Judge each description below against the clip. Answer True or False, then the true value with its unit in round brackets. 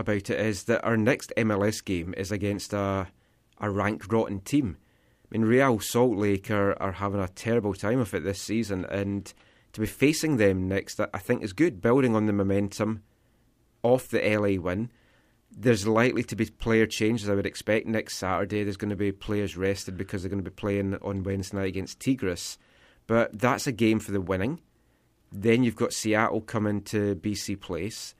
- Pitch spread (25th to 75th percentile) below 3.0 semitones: True (2.5 semitones)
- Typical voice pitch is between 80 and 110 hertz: True (105 Hz)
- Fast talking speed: False (195 wpm)